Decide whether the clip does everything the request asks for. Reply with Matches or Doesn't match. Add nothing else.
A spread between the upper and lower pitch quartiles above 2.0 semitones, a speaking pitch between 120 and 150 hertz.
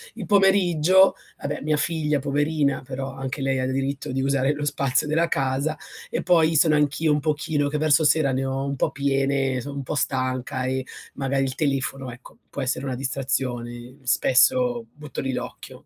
Matches